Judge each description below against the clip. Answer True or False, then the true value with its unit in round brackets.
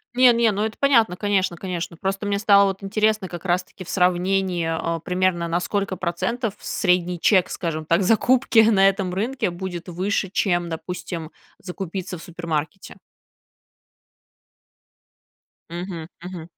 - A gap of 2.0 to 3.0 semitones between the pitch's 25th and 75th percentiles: True (2.7 semitones)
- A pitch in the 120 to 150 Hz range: False (185 Hz)